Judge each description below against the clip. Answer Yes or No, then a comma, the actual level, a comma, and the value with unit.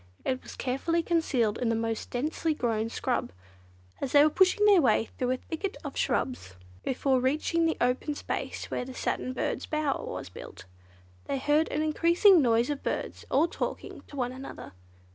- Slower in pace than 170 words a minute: No, average, 180 wpm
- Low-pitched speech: No, very high, 275 Hz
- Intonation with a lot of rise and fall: No, average, 4.3 semitones